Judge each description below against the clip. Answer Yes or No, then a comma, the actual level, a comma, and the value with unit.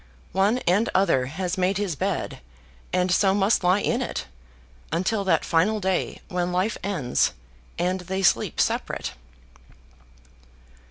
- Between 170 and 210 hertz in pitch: Yes, medium, 185 Hz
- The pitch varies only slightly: Yes, narrow, 1.8 semitones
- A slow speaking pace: Yes, slow, 130 wpm